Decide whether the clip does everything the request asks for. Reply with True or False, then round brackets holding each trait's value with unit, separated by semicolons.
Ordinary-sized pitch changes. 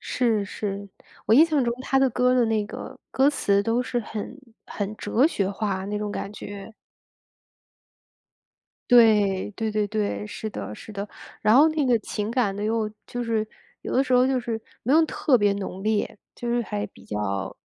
True (3.3 semitones)